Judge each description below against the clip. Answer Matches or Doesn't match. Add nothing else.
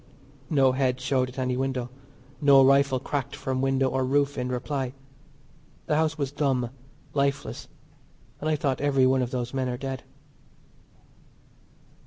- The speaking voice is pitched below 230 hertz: Matches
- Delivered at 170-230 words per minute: Doesn't match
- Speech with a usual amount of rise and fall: Doesn't match